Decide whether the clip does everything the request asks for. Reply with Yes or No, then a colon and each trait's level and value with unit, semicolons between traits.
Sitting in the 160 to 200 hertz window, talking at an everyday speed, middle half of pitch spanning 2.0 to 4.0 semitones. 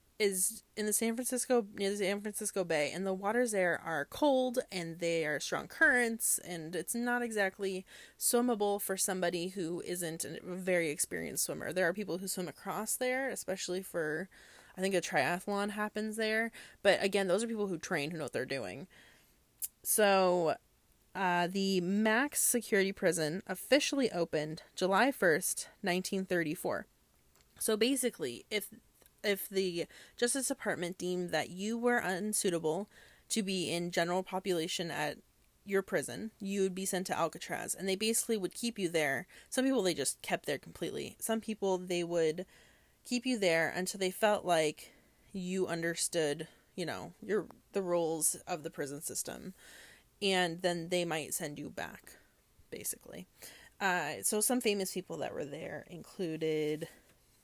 Yes: high, 190 Hz; average, 160 wpm; average, 3.6 semitones